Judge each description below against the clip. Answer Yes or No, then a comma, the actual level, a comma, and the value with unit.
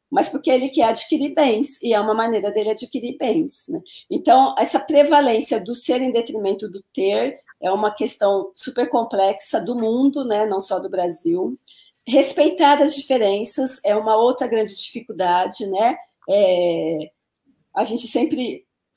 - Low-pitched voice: No, high, 235 Hz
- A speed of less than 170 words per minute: Yes, average, 150 wpm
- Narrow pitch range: No, average, 5.3 semitones